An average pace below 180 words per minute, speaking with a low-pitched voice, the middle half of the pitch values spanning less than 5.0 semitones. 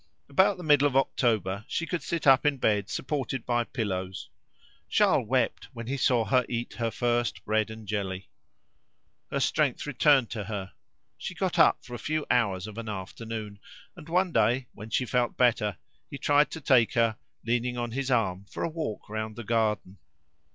No: average, 185 wpm; low, 120 Hz; average, 4.0 semitones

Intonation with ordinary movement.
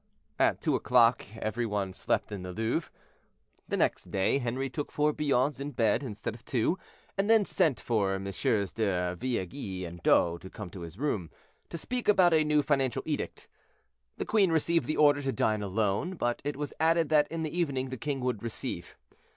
No: wide, 6.5 semitones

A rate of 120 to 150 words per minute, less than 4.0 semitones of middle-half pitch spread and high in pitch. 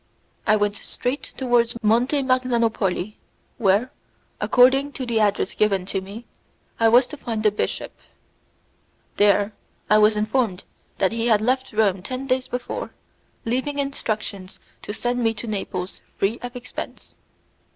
Yes: average, 140 wpm; average, 3.4 semitones; high, 225 Hz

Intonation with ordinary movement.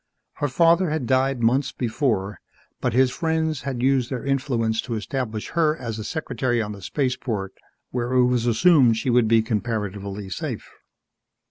Yes: average, 3.6 semitones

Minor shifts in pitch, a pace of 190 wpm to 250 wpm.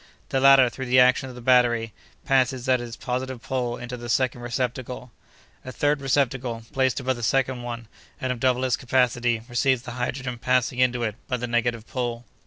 Yes: narrow, 1.4 semitones; average, 195 wpm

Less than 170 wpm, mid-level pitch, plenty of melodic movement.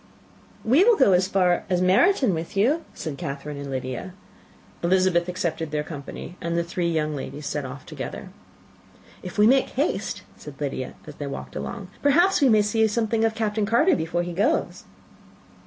No: average, 175 wpm; medium, 180 Hz; wide, 6.5 semitones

